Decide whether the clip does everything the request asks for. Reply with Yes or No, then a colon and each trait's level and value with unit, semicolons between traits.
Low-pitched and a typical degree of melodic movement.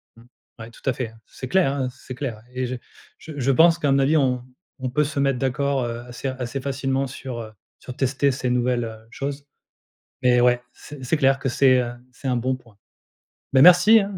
No: low, 130 Hz; narrow, 2.1 semitones